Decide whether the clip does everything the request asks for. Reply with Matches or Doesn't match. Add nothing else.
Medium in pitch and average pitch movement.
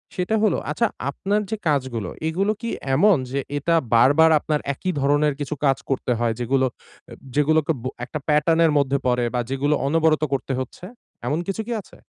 Matches